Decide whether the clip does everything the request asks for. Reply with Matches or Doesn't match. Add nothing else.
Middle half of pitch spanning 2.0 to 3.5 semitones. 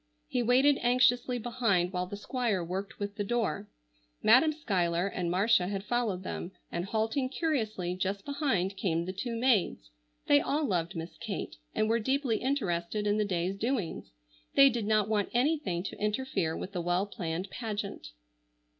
Doesn't match